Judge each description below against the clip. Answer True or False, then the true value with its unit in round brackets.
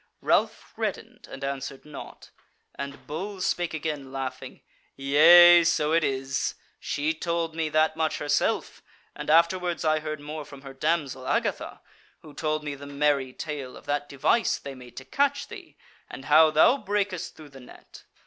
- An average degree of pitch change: True (3.2 semitones)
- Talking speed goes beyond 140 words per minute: True (165 wpm)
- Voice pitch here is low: False (150 Hz)